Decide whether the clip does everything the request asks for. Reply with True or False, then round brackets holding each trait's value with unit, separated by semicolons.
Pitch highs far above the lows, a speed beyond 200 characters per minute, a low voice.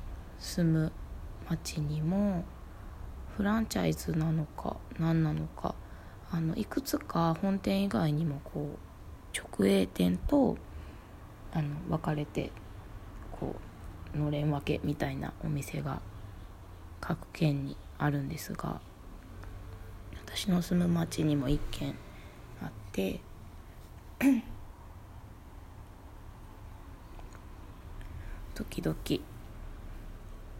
False (8.8 semitones; 150 characters per minute; 100 Hz)